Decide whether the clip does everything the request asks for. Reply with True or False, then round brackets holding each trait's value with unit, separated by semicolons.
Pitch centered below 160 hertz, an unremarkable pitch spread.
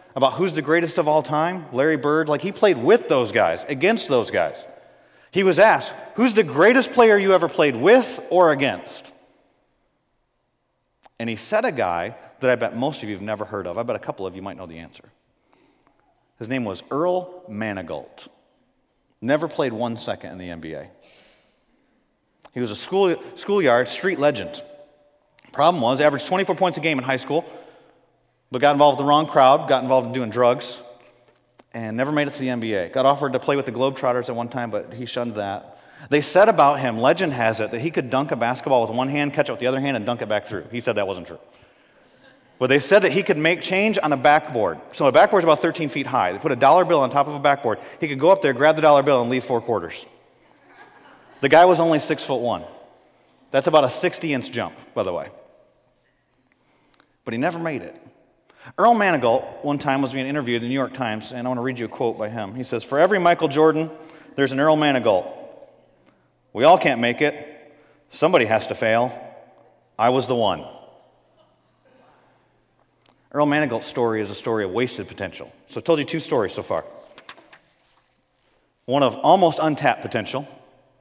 True (140 Hz; 4.5 semitones)